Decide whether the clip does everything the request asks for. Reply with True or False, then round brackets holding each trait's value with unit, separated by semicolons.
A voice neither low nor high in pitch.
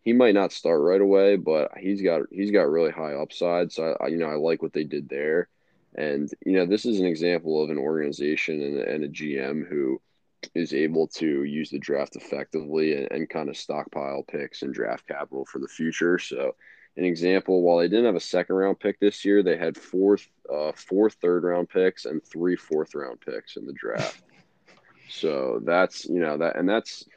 False (85 Hz)